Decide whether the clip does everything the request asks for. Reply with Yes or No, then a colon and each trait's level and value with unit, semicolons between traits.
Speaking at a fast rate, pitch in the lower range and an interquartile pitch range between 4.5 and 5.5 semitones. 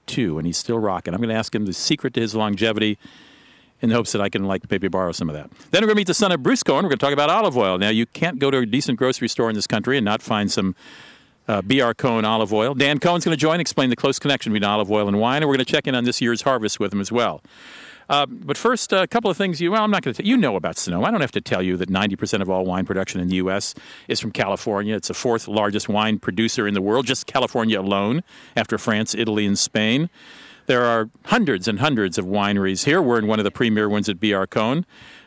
Yes: fast, 295 wpm; low, 110 Hz; average, 5.1 semitones